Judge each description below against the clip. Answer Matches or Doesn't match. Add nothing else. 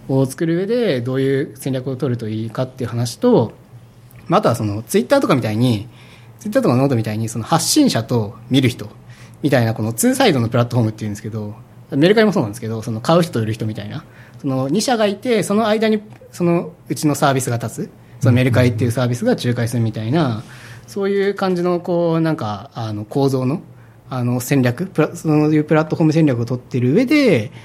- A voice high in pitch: Doesn't match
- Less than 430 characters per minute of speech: Doesn't match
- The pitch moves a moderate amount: Doesn't match